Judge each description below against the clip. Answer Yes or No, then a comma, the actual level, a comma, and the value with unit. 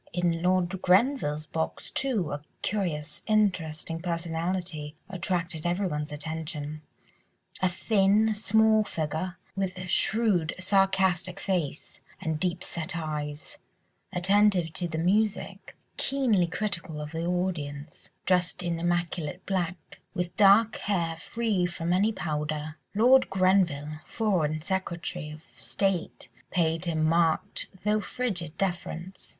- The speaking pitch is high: No, medium, 175 Hz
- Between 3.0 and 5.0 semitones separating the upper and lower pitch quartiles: Yes, average, 3.4 semitones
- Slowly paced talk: Yes, slow, 110 wpm